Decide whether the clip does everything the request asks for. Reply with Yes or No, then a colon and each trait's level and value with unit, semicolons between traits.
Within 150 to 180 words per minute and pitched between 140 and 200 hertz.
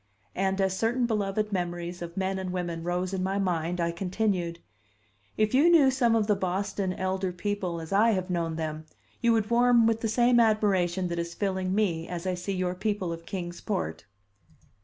No: average, 195 wpm; high, 190 Hz